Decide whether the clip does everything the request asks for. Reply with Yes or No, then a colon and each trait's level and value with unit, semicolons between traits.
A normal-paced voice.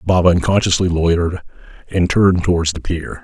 Yes: average, 150 wpm